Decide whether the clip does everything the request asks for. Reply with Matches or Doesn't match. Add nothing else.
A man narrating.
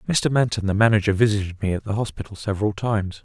Matches